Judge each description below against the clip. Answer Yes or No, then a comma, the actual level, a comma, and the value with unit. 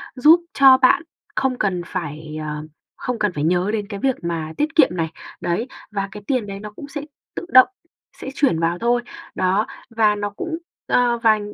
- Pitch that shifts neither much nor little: No, wide, 6.3 semitones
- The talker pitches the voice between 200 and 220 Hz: Yes, high, 210 Hz